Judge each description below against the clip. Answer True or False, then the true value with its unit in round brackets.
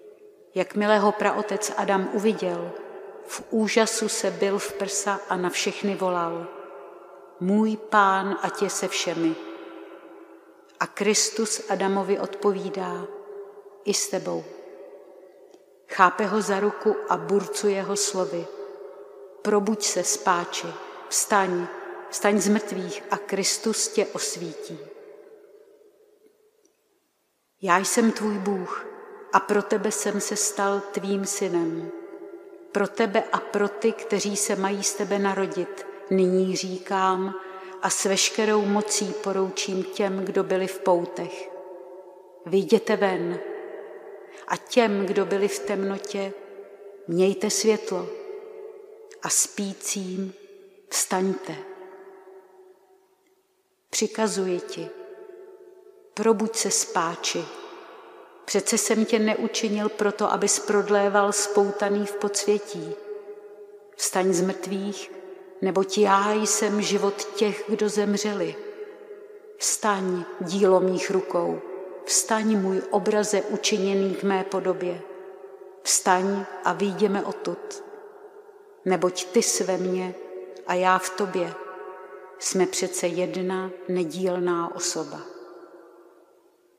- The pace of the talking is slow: True (100 wpm)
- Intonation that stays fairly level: True (2.3 semitones)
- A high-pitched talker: True (200 Hz)